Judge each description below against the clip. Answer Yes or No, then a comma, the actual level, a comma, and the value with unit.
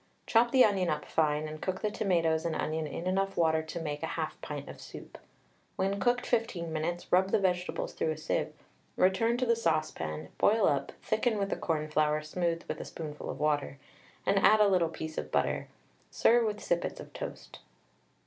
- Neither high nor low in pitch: Yes, medium, 170 Hz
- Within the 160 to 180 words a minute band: No, average, 190 wpm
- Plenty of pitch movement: No, average, 4.3 semitones